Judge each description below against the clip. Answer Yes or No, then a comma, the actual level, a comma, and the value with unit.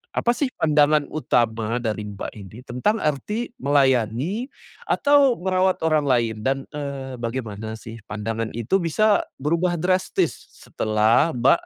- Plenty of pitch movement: Yes, wide, 7.3 semitones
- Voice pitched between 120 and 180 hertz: Yes, low, 135 Hz